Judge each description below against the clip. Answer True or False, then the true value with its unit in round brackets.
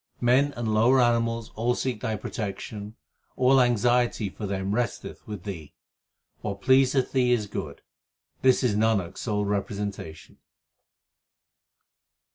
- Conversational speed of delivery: False (130 wpm)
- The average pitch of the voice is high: False (110 Hz)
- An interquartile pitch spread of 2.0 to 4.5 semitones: True (3.3 semitones)